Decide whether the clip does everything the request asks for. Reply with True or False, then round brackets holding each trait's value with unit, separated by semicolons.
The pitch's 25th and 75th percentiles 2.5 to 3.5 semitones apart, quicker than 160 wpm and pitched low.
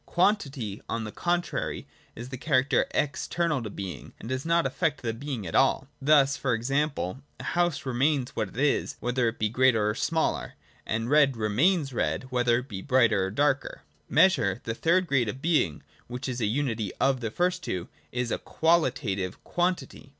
False (4.7 semitones; 185 wpm; 130 Hz)